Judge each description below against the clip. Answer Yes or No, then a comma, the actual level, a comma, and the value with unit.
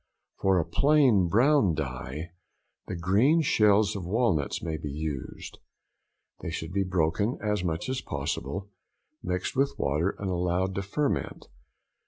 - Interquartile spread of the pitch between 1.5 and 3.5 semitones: No, average, 4.8 semitones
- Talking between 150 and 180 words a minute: No, average, 140 wpm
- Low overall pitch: Yes, very low, 95 Hz